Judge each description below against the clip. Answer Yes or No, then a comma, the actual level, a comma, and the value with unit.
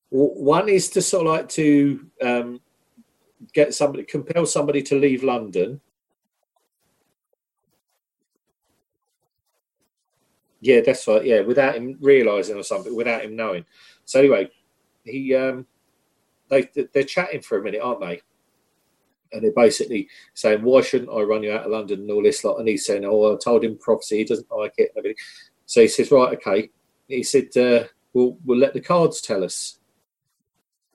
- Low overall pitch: No, medium, 145 Hz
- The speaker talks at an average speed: Yes, average, 160 wpm